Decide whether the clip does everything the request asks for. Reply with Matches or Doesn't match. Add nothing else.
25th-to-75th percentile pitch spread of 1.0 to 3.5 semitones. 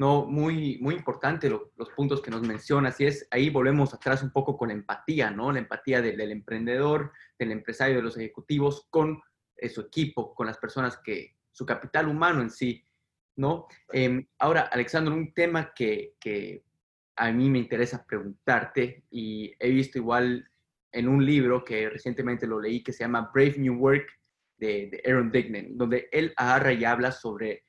Matches